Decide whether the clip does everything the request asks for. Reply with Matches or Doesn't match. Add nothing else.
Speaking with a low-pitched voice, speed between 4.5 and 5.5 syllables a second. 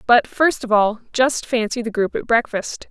Doesn't match